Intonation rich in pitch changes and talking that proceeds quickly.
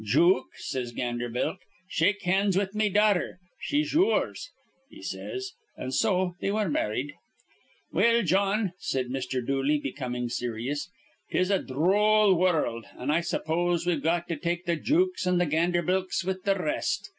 No: wide, 6.0 semitones; average, 155 wpm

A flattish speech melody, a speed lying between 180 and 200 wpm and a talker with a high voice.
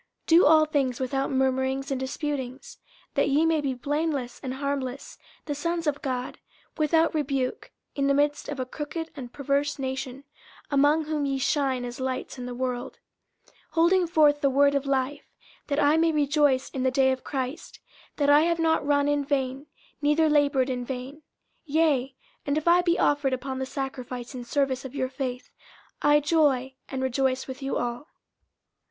Yes: narrow, 2.1 semitones; average, 185 wpm; very high, 275 Hz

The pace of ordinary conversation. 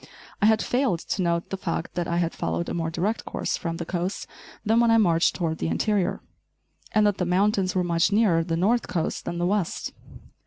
No: fast, 220 wpm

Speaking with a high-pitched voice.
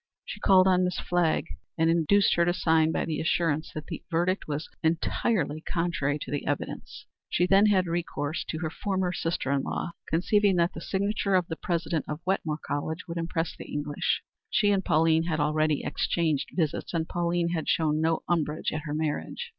No: medium, 165 Hz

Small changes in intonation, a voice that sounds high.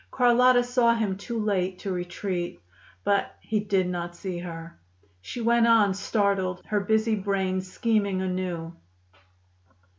No: average, 3.2 semitones; high, 200 Hz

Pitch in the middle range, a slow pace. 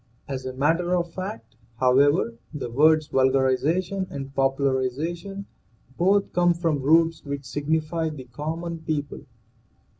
Yes: medium, 150 Hz; slow, 120 wpm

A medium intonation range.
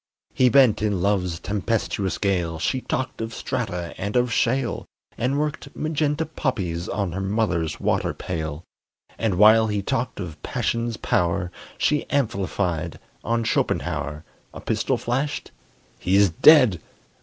No: wide, 5.7 semitones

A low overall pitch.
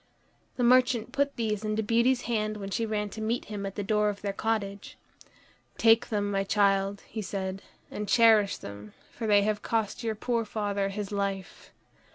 No: high, 210 Hz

